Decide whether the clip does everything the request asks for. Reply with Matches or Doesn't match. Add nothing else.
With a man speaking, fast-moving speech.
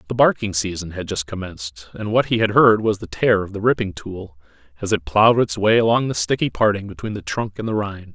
Matches